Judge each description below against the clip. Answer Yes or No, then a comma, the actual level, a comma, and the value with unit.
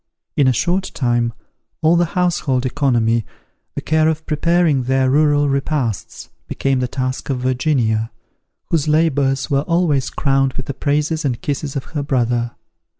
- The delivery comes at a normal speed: Yes, average, 150 wpm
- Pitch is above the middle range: No, medium, 140 Hz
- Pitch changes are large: No, average, 3.3 semitones